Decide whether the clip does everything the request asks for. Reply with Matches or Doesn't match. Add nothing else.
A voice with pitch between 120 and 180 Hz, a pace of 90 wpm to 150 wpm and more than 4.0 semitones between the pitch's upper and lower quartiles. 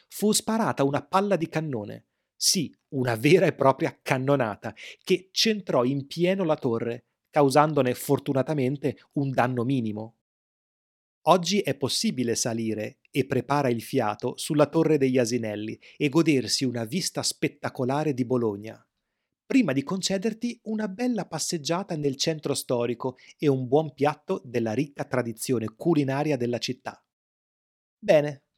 Matches